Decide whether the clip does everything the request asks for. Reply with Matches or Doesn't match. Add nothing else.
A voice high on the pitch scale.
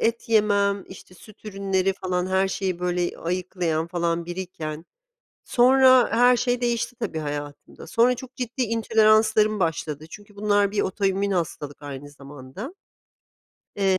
Matches